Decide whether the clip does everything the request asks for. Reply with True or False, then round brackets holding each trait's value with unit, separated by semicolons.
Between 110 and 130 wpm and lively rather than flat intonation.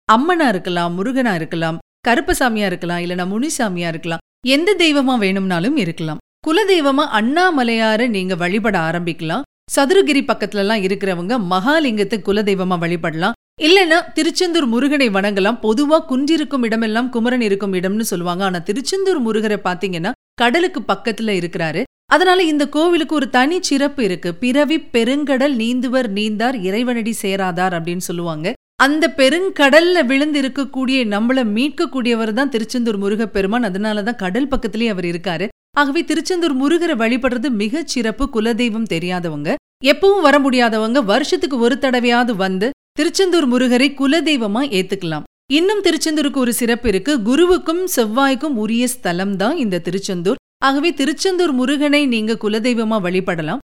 True (125 wpm; 6.4 semitones)